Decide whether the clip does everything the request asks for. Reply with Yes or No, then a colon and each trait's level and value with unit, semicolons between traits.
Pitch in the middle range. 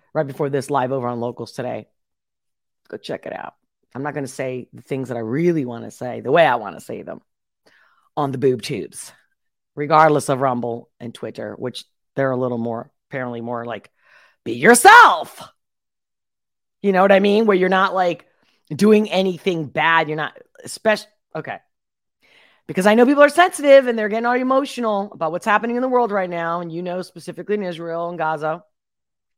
Yes: medium, 170 Hz